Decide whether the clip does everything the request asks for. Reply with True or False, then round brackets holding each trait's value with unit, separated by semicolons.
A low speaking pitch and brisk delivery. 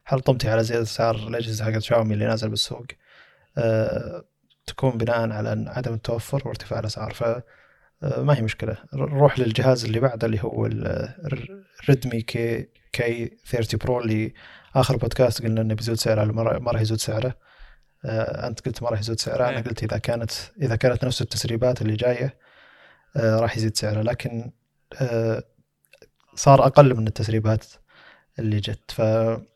True (115 Hz; 150 wpm)